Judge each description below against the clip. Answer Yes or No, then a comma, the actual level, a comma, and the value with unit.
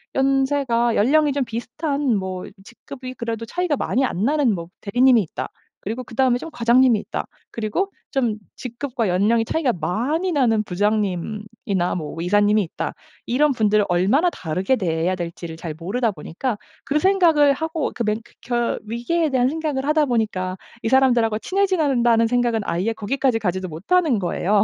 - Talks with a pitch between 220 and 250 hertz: Yes, high, 235 Hz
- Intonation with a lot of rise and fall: No, average, 5.0 semitones